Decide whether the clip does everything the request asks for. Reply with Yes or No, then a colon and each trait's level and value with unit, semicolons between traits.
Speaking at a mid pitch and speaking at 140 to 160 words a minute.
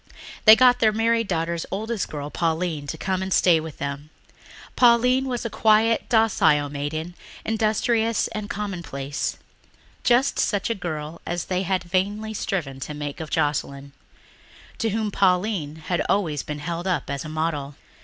Yes: medium, 180 Hz; average, 155 wpm